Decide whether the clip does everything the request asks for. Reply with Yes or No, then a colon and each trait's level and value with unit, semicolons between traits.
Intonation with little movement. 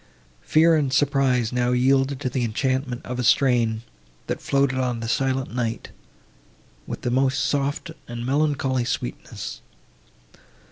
Yes: narrow, 2.1 semitones